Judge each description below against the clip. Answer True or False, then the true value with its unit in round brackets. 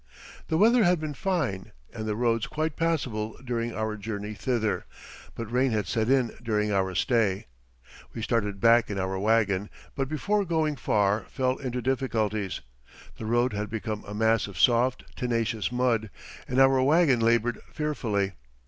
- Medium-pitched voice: False (115 Hz)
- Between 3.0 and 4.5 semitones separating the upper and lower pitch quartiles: True (3.7 semitones)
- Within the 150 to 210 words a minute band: True (160 wpm)